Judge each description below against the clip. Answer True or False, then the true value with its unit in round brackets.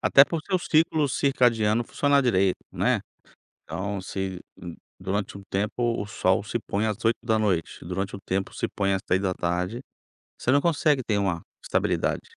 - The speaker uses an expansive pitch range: False (4.5 semitones)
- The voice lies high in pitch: False (105 Hz)